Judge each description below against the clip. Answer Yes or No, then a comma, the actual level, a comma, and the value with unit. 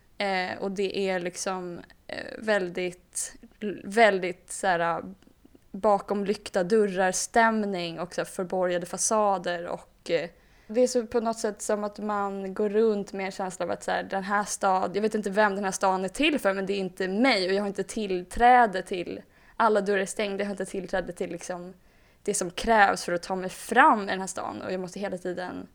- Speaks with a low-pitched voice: No, high, 195 Hz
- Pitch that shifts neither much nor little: No, narrow, 2.3 semitones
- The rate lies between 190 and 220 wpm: Yes, fast, 195 wpm